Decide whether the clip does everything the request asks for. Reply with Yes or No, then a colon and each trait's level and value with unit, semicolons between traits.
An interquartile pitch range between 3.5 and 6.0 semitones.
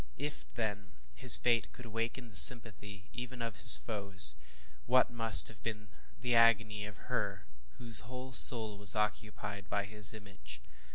No: narrow, 2.4 semitones